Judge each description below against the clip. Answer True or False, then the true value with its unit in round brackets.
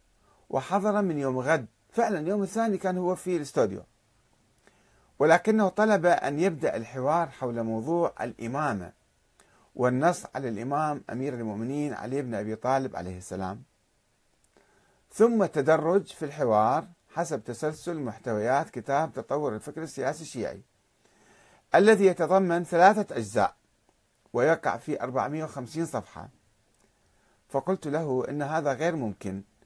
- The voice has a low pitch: False (145 Hz)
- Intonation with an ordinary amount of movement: False (7.2 semitones)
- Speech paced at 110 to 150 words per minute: True (115 wpm)